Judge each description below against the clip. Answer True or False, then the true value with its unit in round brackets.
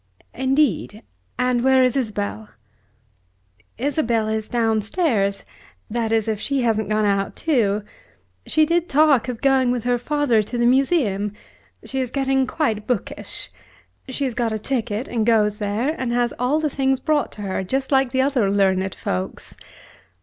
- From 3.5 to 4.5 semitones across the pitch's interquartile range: True (3.9 semitones)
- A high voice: True (240 Hz)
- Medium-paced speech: True (160 wpm)